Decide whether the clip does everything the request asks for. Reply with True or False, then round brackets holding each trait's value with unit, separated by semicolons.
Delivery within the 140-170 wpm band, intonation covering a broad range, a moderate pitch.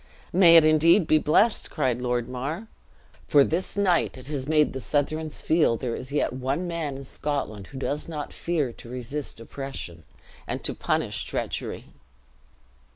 False (160 wpm; 3.8 semitones; 145 Hz)